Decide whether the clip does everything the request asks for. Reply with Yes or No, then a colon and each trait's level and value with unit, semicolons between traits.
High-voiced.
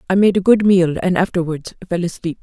No: medium, 180 Hz